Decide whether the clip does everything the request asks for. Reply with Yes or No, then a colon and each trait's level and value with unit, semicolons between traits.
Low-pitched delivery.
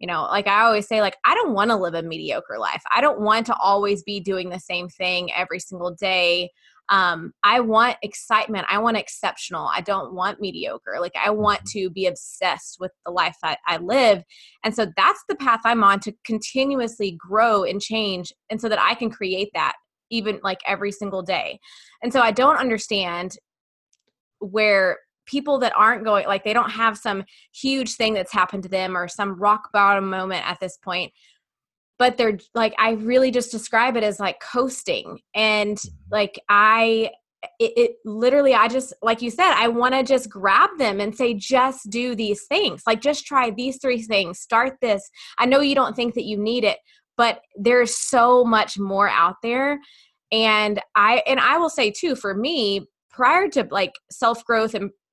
No: high, 215 Hz